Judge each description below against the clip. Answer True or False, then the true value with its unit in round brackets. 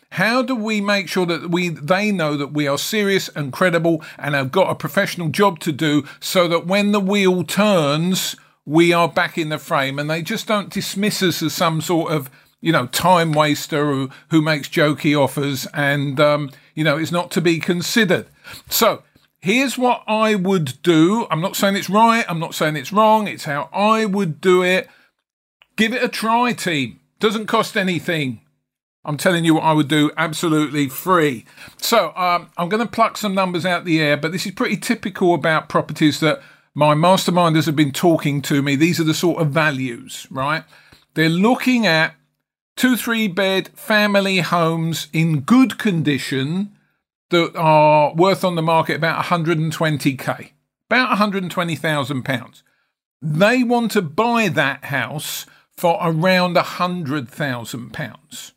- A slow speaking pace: False (170 wpm)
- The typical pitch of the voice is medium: True (170 Hz)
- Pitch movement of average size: True (4.3 semitones)